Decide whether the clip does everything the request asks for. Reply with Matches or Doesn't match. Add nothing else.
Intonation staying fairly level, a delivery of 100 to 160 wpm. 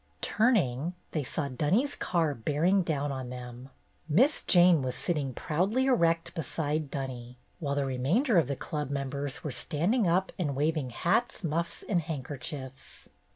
Doesn't match